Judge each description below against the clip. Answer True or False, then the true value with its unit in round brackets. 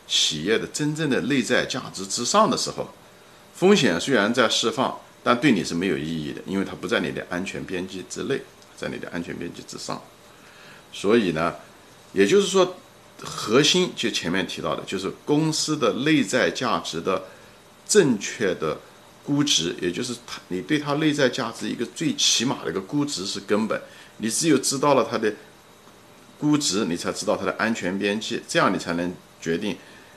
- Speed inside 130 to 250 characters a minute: False (265 characters per minute)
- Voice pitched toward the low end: True (125 Hz)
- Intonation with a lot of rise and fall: True (7.8 semitones)